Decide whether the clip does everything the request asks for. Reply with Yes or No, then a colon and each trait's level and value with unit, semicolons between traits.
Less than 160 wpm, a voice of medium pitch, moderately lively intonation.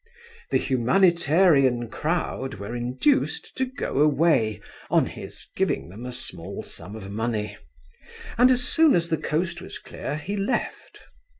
No: average, 140 wpm; medium, 150 Hz; wide, 7.4 semitones